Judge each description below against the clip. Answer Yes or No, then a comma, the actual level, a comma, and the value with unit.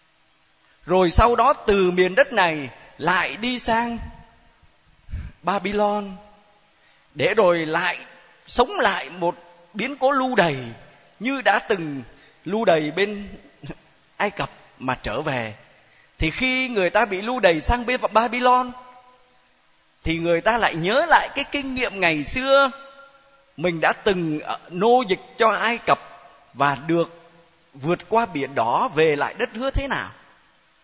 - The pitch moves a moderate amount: No, wide, 7.3 semitones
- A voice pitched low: No, high, 200 Hz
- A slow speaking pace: Yes, slow, 140 wpm